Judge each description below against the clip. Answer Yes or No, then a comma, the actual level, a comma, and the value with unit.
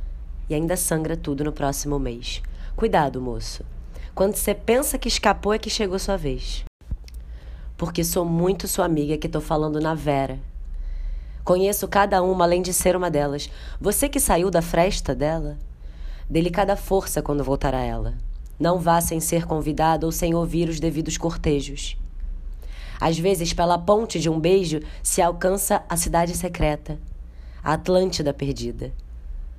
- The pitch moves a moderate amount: No, wide, 8.1 semitones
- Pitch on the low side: No, medium, 160 Hz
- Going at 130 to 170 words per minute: Yes, average, 150 wpm